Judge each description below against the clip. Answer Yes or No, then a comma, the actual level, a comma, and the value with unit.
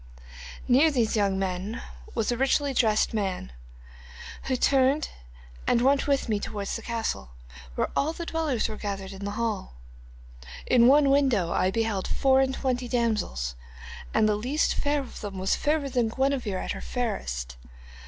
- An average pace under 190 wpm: Yes, average, 165 wpm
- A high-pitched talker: Yes, high, 225 Hz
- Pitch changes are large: Yes, wide, 5.7 semitones